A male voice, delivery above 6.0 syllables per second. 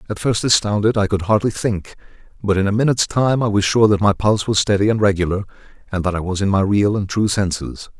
Yes: male; 6.2 syllables/s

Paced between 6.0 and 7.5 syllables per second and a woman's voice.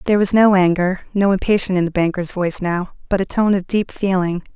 Yes: 6.1 syllables/s; female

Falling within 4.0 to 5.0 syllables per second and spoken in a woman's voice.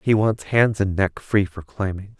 No: 4.3 syllables/s; male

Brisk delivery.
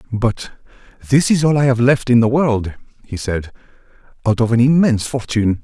No: average, 180 wpm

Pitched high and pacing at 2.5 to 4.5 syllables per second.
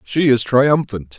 No: low, 125 Hz; 3.7 syllables/s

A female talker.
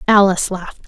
Yes: female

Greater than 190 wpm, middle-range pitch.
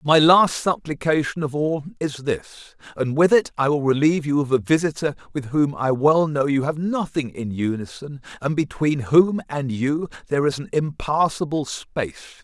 No: average, 180 wpm; medium, 145 Hz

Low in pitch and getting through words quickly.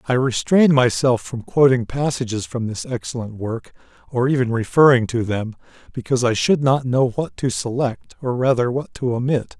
No: low, 125 Hz; average, 175 wpm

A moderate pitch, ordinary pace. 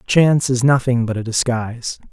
No: low, 125 Hz; average, 170 wpm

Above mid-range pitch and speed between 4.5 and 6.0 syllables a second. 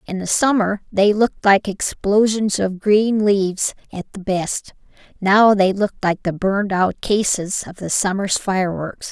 No: high, 195 Hz; 4.3 syllables/s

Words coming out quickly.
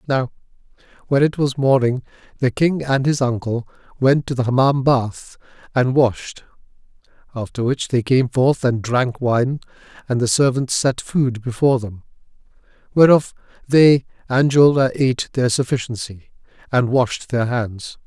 No: average, 145 wpm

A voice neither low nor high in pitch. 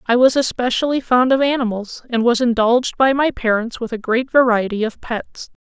No: high, 240 Hz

